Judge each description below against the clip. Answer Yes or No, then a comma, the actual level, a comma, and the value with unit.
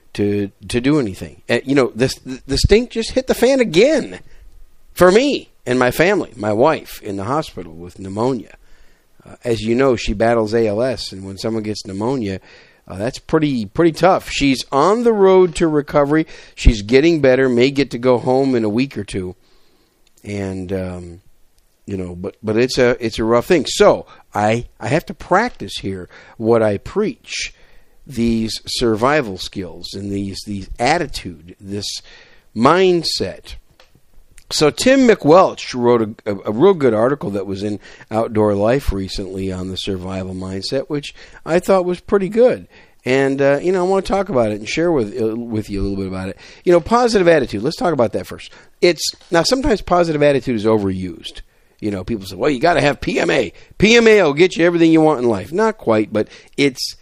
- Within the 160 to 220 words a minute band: Yes, average, 190 wpm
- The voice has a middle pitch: No, low, 115 Hz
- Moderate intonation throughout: No, wide, 7.3 semitones